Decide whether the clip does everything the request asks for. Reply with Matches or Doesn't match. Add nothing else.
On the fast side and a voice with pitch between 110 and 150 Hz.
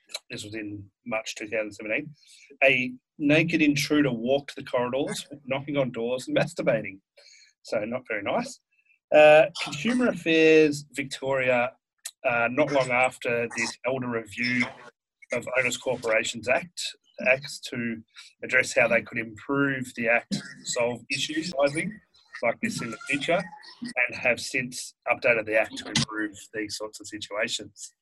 Doesn't match